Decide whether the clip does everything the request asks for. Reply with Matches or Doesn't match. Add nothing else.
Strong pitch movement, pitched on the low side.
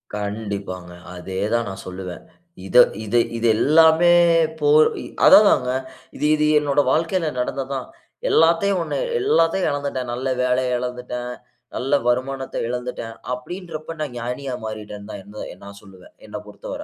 Matches